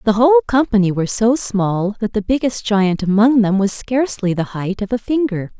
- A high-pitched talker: Yes, high, 215 Hz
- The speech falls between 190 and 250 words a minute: Yes, fast, 205 wpm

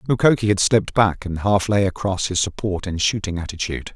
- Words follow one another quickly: No, average, 195 wpm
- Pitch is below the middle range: Yes, low, 100 Hz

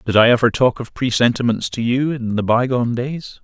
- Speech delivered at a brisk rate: Yes, fast, 210 wpm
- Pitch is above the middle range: No, low, 120 Hz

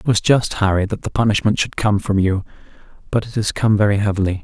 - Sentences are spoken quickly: Yes, fast, 230 wpm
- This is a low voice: Yes, low, 105 Hz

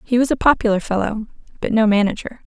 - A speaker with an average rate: Yes, average, 190 wpm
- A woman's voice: Yes, female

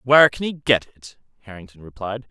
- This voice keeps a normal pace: Yes, average, 180 wpm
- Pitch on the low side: Yes, low, 115 Hz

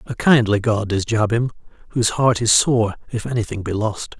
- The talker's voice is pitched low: Yes, low, 110 Hz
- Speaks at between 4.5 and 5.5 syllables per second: Yes, 5.2 syllables/s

